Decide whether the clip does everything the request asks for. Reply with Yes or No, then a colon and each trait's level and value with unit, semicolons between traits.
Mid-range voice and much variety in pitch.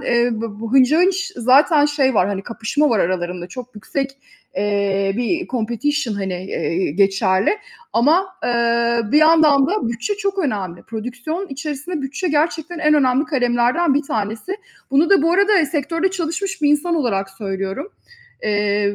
No: very high, 255 Hz; wide, 7.0 semitones